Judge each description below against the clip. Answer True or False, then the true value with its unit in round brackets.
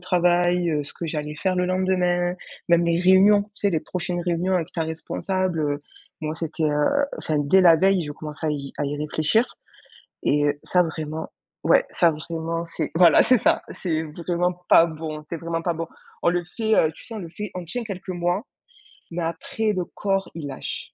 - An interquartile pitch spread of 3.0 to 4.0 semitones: False (2.6 semitones)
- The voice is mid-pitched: True (170 Hz)